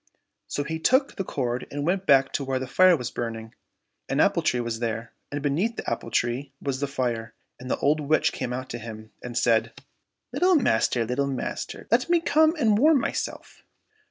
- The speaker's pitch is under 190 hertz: Yes, low, 135 Hz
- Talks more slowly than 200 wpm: No, fast, 205 wpm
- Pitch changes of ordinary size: No, wide, 7.1 semitones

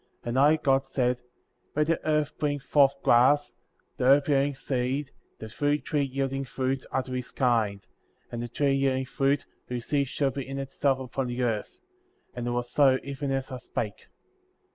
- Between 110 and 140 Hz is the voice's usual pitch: Yes, low, 135 Hz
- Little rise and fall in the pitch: Yes, narrow, 2.1 semitones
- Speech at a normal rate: Yes, average, 185 wpm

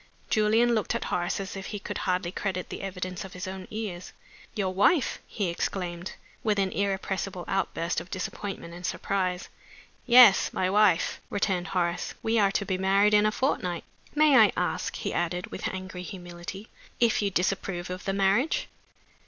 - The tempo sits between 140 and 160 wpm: No, average, 170 wpm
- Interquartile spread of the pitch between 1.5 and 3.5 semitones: Yes, narrow, 2.5 semitones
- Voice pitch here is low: No, high, 190 Hz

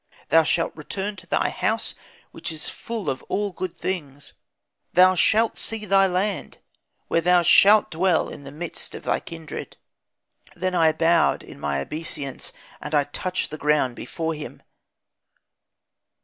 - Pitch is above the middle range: No, medium, 165 Hz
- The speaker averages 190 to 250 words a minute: No, average, 150 wpm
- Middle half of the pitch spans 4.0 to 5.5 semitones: No, average, 3.6 semitones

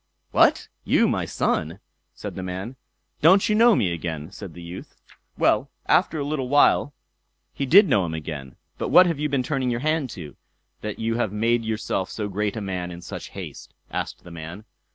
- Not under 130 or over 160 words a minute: No, average, 195 wpm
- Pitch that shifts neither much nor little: No, wide, 7.9 semitones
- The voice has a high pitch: No, low, 105 Hz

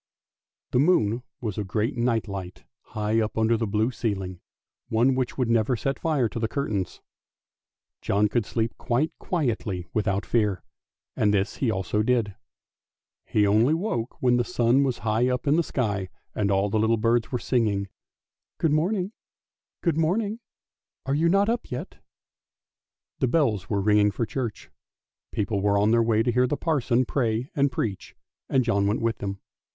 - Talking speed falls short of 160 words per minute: No, average, 175 wpm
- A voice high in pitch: No, low, 115 Hz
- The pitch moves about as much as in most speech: Yes, average, 3.8 semitones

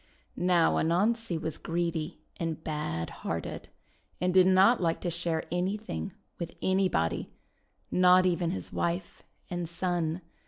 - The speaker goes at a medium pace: No, slow, 130 wpm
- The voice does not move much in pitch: Yes, narrow, 2.0 semitones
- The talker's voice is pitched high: No, medium, 175 Hz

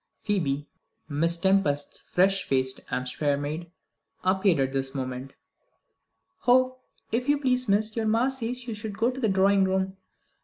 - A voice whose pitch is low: No, high, 190 Hz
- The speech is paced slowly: No, average, 150 wpm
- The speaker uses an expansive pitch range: Yes, wide, 7.8 semitones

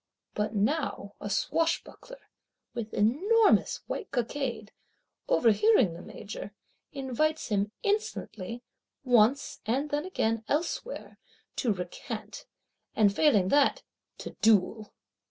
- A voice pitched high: Yes, high, 240 Hz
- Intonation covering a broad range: Yes, wide, 6.4 semitones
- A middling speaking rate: No, slow, 100 wpm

